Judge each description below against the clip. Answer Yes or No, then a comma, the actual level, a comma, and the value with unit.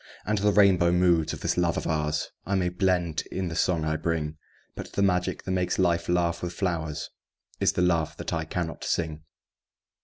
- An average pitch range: No, narrow, 2.1 semitones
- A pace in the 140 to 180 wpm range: No, average, 195 wpm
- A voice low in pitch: Yes, very low, 85 Hz